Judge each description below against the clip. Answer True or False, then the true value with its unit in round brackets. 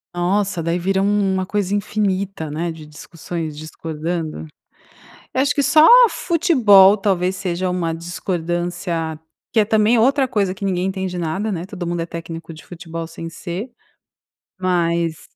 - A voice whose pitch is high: False (180 Hz)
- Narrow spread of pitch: False (3.1 semitones)